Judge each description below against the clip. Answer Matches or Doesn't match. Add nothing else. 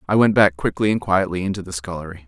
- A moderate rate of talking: Doesn't match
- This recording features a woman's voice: Doesn't match